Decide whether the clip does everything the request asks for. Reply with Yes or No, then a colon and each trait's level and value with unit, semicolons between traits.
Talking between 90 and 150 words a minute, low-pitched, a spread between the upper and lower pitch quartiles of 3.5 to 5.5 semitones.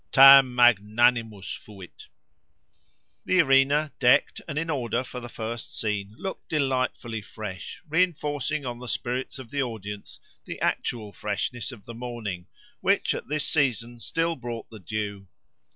Yes: average, 145 wpm; low, 120 Hz; average, 4.2 semitones